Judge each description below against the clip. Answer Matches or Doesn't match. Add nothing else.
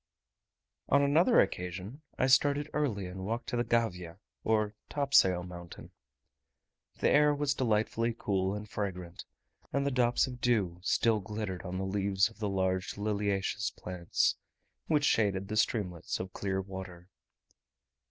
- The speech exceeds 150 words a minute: Doesn't match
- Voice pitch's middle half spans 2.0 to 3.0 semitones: Doesn't match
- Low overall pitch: Matches